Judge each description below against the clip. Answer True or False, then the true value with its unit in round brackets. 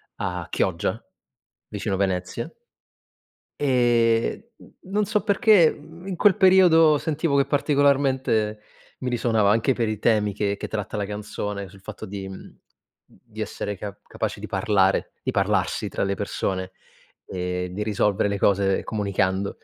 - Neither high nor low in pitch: False (105 Hz)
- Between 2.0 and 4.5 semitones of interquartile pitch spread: False (6.1 semitones)